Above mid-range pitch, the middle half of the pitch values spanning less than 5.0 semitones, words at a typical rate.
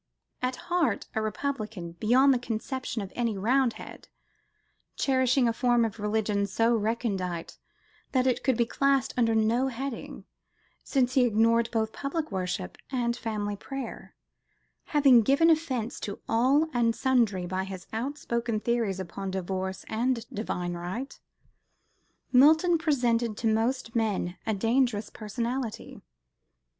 No: high, 230 Hz; average, 3.6 semitones; slow, 130 wpm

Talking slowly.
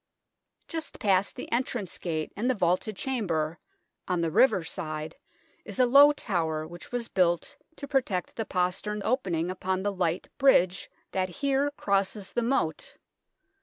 No: average, 150 wpm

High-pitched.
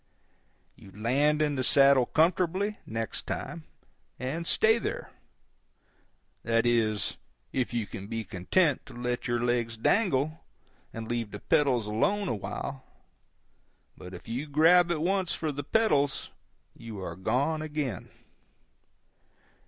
No: low, 135 Hz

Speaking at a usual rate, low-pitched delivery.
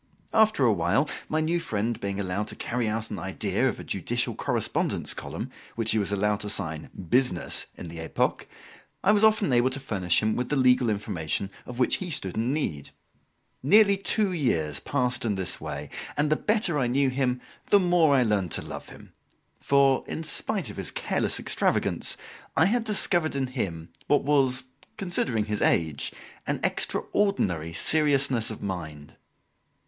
Yes: average, 175 wpm; low, 125 Hz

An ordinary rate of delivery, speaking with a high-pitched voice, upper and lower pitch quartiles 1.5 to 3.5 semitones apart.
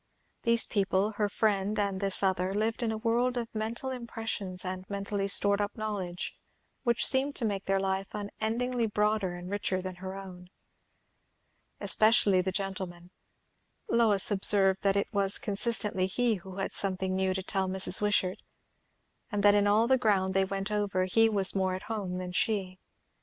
Yes: average, 170 wpm; high, 200 Hz; narrow, 2.4 semitones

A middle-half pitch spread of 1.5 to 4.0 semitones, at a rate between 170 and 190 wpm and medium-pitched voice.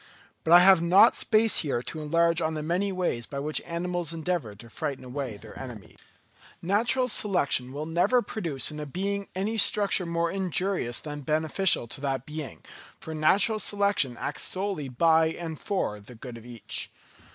No: wide, 5.5 semitones; average, 175 wpm; medium, 160 Hz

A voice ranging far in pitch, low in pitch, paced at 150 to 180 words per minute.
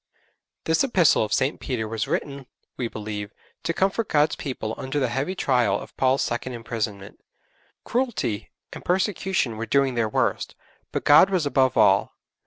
Yes: wide, 6.1 semitones; low, 130 Hz; average, 160 wpm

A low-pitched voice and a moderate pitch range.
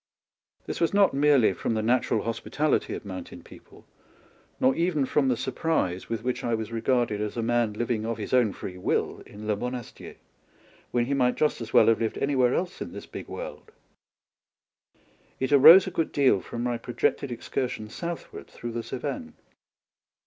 Yes: low, 120 Hz; average, 3.9 semitones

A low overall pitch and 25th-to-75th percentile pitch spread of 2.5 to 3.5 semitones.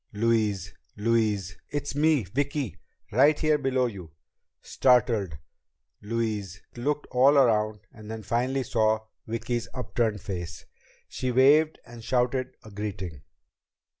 No: low, 115 Hz; average, 4.0 semitones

